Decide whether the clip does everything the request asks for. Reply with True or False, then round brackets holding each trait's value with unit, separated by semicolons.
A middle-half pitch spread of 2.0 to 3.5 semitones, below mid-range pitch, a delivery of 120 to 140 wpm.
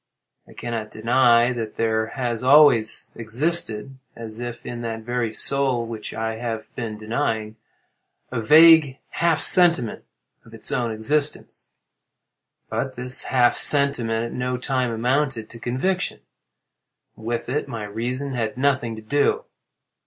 True (3.1 semitones; 120 Hz; 135 wpm)